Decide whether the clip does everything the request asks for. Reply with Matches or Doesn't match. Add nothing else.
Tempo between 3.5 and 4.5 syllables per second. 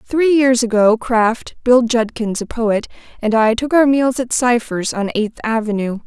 Matches